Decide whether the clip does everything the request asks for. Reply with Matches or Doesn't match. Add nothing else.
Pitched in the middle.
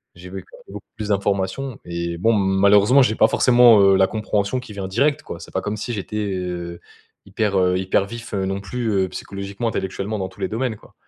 Doesn't match